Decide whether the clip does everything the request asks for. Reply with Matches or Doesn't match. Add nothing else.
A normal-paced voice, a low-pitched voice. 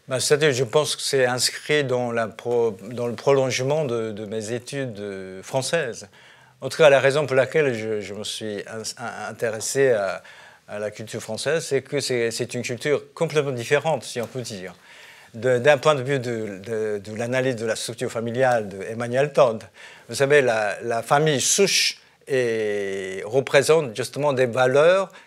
Matches